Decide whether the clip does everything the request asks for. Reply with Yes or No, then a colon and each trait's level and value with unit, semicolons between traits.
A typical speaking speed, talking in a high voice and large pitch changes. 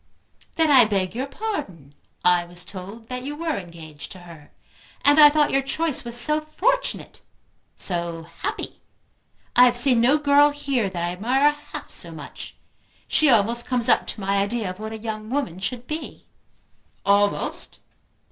Yes: average, 165 wpm; high, 235 Hz; wide, 7.3 semitones